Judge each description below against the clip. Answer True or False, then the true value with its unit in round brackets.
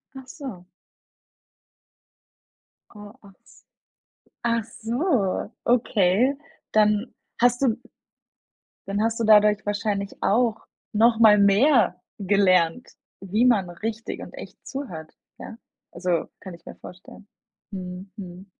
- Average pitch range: True (3.3 semitones)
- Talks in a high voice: True (210 Hz)